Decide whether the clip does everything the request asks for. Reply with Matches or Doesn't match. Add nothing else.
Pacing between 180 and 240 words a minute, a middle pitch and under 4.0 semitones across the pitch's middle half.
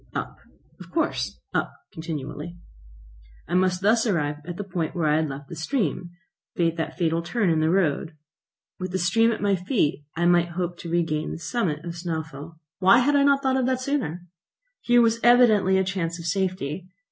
Doesn't match